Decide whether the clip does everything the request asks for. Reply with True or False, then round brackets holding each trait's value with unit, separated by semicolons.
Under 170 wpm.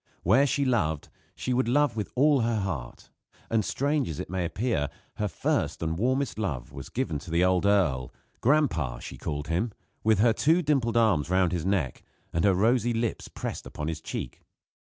False (190 wpm)